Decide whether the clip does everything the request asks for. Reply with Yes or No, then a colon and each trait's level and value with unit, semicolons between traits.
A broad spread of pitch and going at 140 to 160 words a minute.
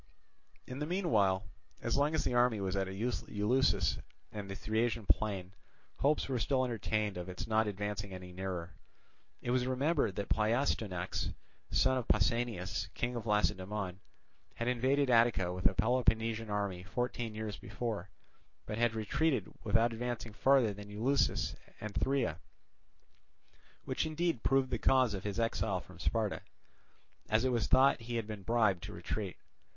No: average, 3.7 semitones; average, 155 wpm